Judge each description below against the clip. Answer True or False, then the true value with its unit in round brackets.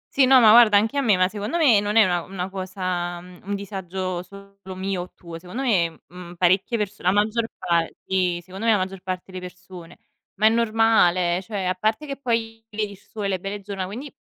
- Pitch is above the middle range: True (195 Hz)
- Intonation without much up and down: False (3.1 semitones)